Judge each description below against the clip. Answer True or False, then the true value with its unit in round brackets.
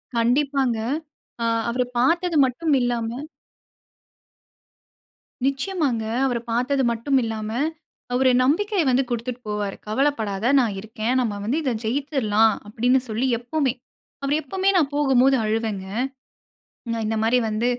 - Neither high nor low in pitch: False (250 Hz)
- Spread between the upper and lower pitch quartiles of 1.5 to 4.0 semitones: True (3.7 semitones)